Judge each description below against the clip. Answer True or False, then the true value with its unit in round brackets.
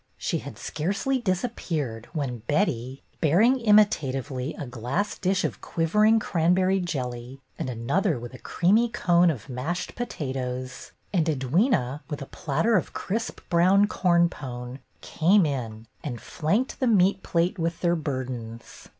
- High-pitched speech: False (165 Hz)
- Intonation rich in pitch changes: True (6.9 semitones)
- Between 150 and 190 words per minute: False (140 wpm)